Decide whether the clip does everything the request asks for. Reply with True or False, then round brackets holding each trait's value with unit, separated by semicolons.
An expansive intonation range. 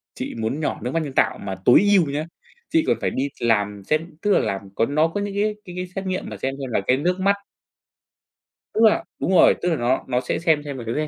True (6.9 semitones)